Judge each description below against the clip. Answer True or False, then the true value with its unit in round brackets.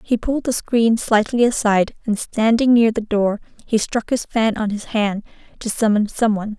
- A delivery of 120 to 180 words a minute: False (200 wpm)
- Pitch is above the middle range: True (220 Hz)